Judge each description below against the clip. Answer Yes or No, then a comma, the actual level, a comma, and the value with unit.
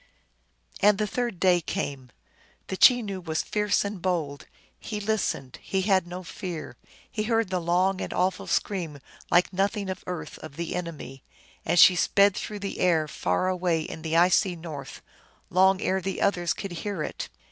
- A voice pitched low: No, medium, 185 Hz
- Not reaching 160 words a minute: No, average, 170 wpm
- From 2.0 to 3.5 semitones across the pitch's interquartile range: Yes, average, 2.9 semitones